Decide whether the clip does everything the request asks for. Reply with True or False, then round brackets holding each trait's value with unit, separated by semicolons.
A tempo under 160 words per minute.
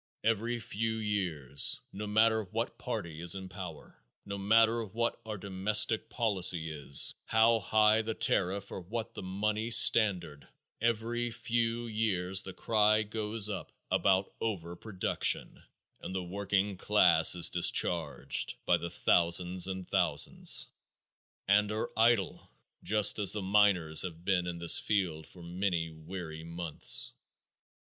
True (135 wpm)